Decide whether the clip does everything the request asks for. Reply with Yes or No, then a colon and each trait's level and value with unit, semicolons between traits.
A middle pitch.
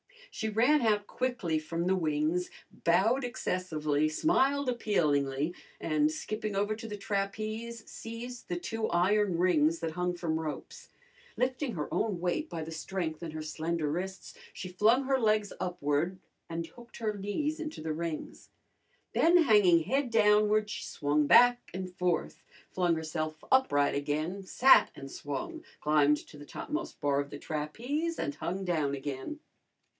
Yes: medium, 180 Hz